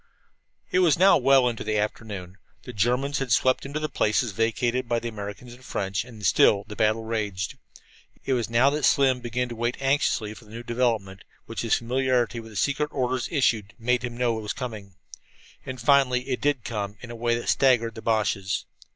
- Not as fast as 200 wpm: No, fast, 205 wpm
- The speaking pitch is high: No, low, 120 Hz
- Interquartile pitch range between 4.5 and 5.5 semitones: No, average, 2.9 semitones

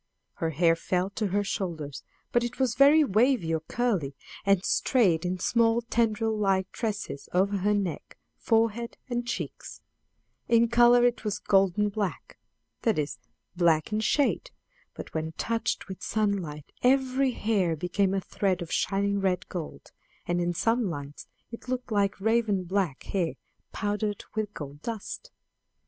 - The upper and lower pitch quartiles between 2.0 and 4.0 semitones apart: No, average, 4.5 semitones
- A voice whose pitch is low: No, high, 200 Hz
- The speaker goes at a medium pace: Yes, average, 150 wpm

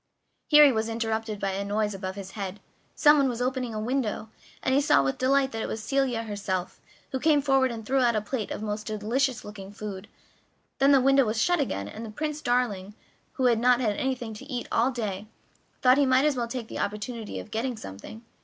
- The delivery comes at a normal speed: No, fast, 220 wpm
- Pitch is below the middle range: No, high, 230 Hz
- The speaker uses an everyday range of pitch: Yes, average, 3.9 semitones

